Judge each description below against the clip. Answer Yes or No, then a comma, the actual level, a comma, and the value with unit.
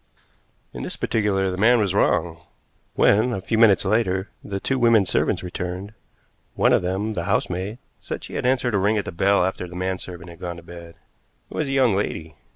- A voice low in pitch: Yes, very low, 95 Hz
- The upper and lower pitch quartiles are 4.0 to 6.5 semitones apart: No, average, 3.5 semitones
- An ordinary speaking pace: No, fast, 210 wpm